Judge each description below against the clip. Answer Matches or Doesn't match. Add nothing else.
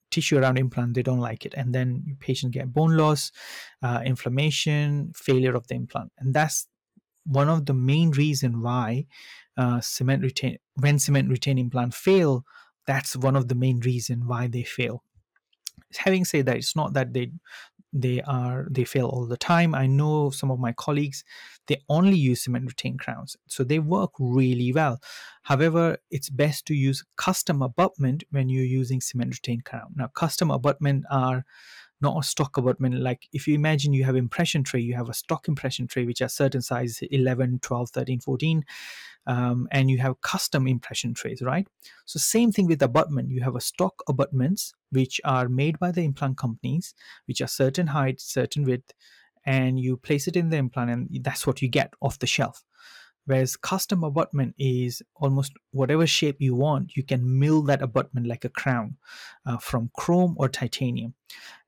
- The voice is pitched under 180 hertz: Matches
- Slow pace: Doesn't match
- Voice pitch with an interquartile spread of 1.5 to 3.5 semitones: Matches